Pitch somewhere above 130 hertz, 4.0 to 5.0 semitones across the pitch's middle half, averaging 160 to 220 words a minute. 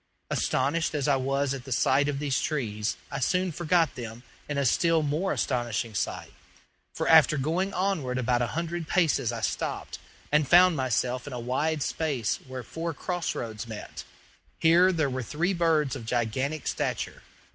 Yes: medium, 140 Hz; average, 4.6 semitones; average, 170 wpm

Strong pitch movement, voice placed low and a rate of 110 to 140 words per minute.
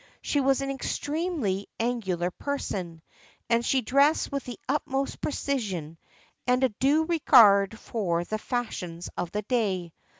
No: wide, 6.4 semitones; high, 235 Hz; slow, 135 wpm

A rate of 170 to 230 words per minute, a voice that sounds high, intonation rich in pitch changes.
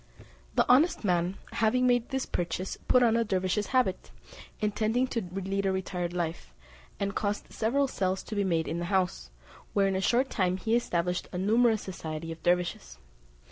No: average, 180 wpm; high, 195 Hz; average, 4.2 semitones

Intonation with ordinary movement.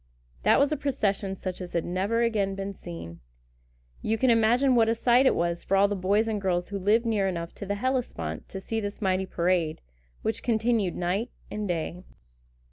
Yes: average, 3.8 semitones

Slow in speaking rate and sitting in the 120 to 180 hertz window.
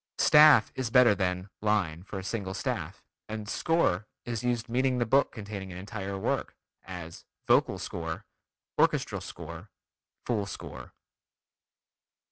No: slow, 130 wpm; low, 105 Hz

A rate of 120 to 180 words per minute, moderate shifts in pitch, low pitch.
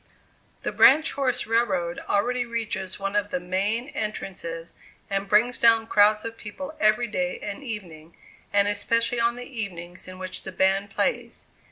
No: average, 160 wpm; average, 3.7 semitones; high, 210 Hz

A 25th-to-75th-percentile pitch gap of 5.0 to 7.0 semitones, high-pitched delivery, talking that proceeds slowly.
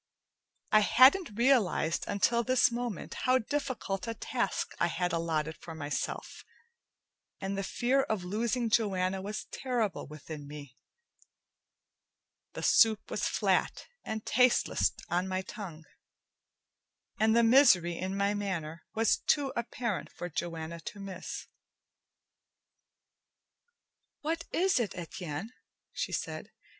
Yes: wide, 5.4 semitones; high, 200 Hz; slow, 120 wpm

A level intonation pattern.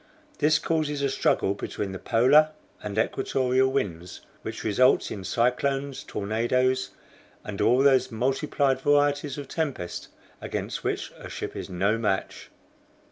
No: average, 4.7 semitones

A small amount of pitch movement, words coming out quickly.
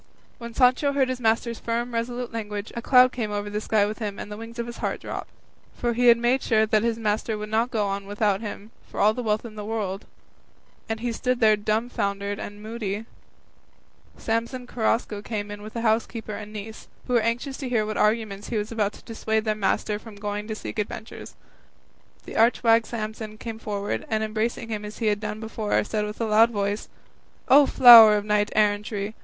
Yes: narrow, 1.9 semitones; fast, 215 wpm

